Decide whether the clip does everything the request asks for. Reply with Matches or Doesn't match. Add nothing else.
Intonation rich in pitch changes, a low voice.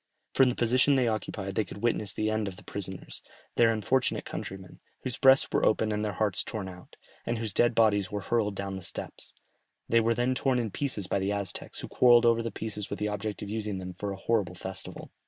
Doesn't match